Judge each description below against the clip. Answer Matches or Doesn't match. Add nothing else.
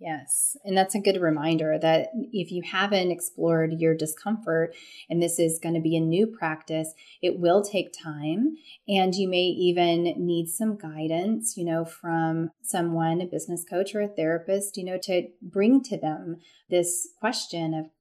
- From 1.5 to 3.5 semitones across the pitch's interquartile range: Matches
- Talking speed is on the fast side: Doesn't match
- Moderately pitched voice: Matches